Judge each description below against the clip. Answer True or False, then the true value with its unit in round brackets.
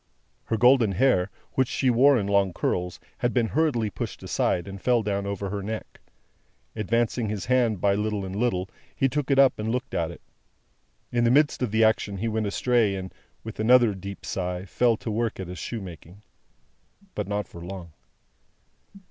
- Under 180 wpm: False (185 wpm)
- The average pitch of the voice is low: True (105 Hz)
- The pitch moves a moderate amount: True (3.7 semitones)